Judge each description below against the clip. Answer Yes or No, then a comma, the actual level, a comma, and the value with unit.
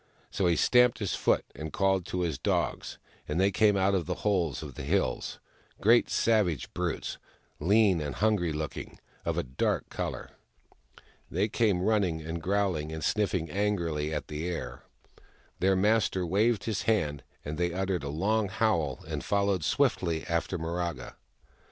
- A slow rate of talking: No, average, 165 wpm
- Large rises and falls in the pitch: No, average, 4.2 semitones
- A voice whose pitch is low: Yes, very low, 90 Hz